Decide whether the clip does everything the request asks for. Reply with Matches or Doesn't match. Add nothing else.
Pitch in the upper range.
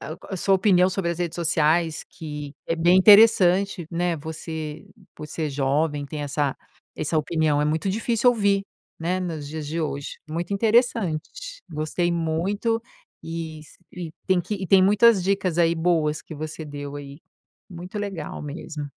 Doesn't match